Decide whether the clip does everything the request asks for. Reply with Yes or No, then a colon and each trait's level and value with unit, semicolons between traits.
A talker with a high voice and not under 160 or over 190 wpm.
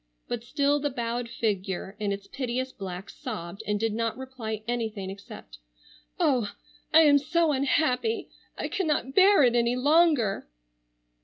No: high, 240 Hz; average, 145 wpm